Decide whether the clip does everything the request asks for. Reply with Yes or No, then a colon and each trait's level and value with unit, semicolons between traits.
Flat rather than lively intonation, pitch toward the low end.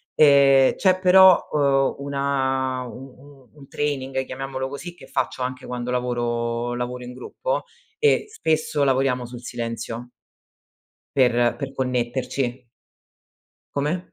Yes: narrow, 2.2 semitones; low, 130 Hz